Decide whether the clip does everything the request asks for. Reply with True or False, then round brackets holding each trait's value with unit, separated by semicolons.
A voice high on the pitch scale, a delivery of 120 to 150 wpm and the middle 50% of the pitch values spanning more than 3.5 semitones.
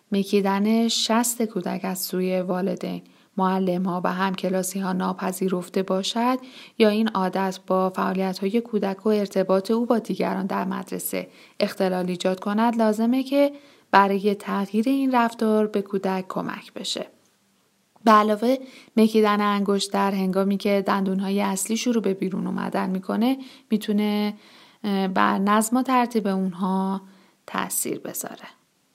False (200 Hz; 135 wpm; 2.8 semitones)